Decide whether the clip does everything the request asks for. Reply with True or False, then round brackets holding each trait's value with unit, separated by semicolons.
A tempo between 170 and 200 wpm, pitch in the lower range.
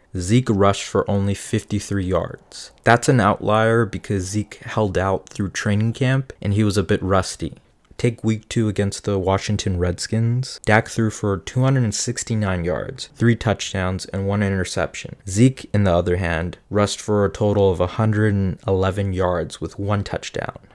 False (155 wpm; 100 Hz)